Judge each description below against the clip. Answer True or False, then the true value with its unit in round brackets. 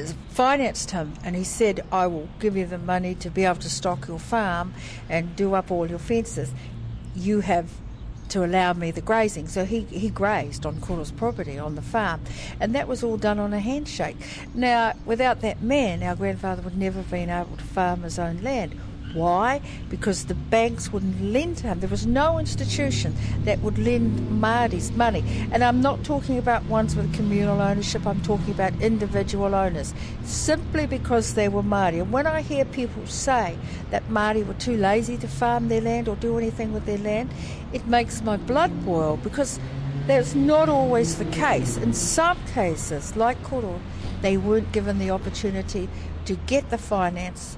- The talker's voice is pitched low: False (185 Hz)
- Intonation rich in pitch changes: True (8.0 semitones)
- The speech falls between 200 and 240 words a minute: False (185 wpm)